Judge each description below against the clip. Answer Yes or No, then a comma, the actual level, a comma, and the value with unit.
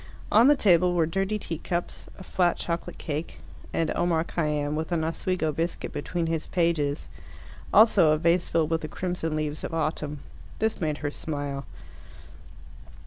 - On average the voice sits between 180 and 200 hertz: No, medium, 165 Hz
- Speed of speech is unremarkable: Yes, average, 155 wpm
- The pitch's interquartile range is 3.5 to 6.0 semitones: No, narrow, 2.5 semitones